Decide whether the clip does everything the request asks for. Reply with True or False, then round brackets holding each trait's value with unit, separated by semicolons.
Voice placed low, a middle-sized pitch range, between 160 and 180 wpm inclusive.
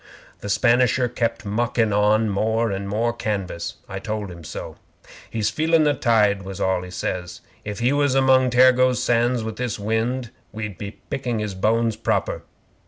True (110 Hz; 3.2 semitones; 170 wpm)